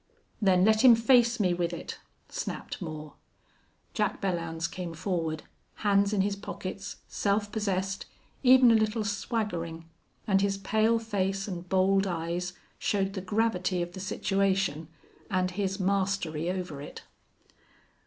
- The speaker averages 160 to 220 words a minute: No, slow, 135 wpm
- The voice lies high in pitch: Yes, high, 195 Hz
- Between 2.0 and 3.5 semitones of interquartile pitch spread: Yes, narrow, 2.6 semitones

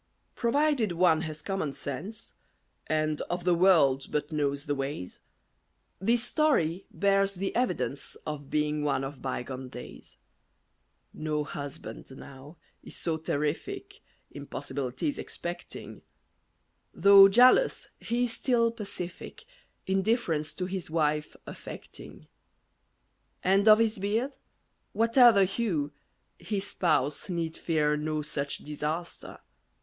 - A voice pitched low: No, medium, 170 Hz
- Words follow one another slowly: Yes, slow, 115 wpm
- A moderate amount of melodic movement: No, wide, 5.7 semitones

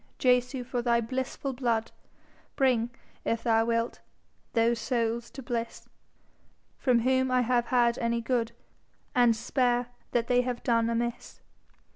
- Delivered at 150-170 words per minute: No, slow, 135 wpm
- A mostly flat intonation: Yes, narrow, 1.3 semitones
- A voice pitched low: No, high, 240 Hz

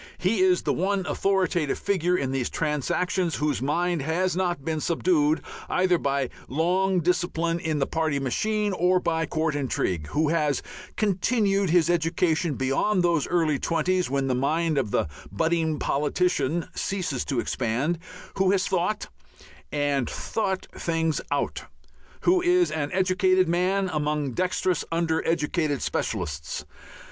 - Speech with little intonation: No, average, 3.9 semitones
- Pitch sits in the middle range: Yes, medium, 165 Hz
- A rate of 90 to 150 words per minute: Yes, average, 140 wpm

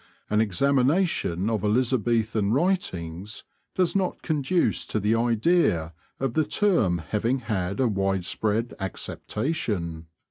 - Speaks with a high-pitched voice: No, low, 110 Hz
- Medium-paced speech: No, slow, 110 wpm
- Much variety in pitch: Yes, wide, 6.1 semitones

